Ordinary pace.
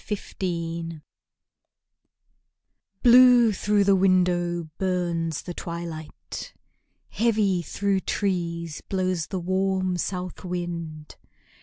No: slow, 90 wpm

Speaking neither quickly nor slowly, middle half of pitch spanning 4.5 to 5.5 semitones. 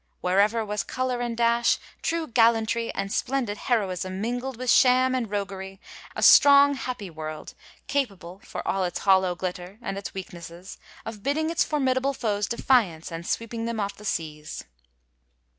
Yes: average, 160 wpm; average, 5.0 semitones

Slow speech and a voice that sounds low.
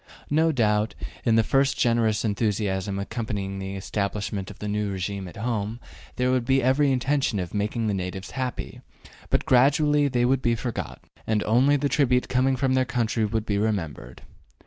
No: average, 175 wpm; low, 115 Hz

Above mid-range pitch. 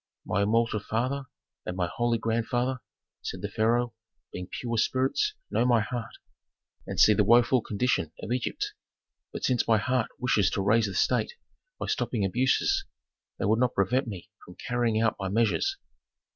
No: low, 115 Hz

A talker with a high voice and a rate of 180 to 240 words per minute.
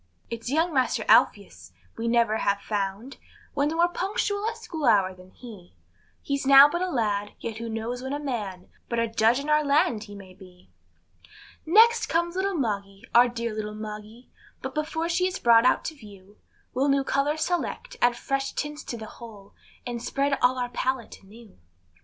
Yes: high, 245 Hz; average, 190 wpm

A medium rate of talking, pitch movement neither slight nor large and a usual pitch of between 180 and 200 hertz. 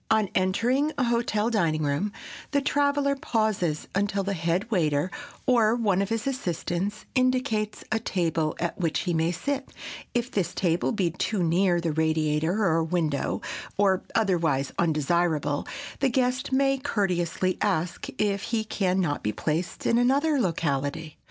No: average, 150 wpm; wide, 5.8 semitones; high, 190 Hz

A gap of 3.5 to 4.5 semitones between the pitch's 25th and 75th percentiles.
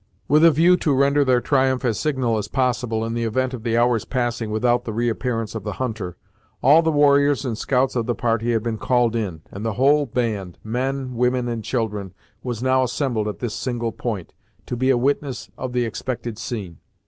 No: narrow, 2.6 semitones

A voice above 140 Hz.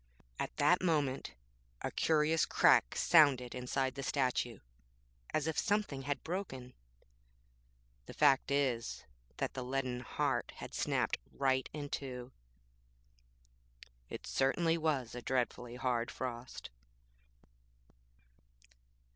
No: low, 135 Hz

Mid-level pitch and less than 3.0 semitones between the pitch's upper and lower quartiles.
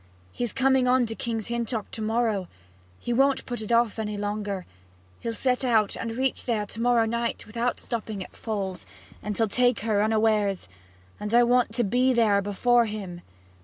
No: high, 225 Hz; narrow, 2.5 semitones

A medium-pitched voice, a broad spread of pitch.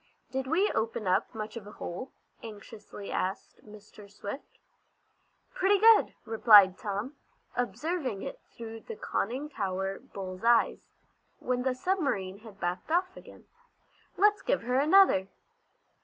No: high, 225 Hz; wide, 6.4 semitones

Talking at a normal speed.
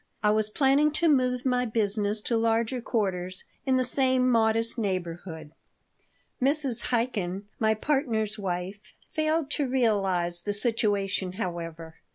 No: slow, 130 wpm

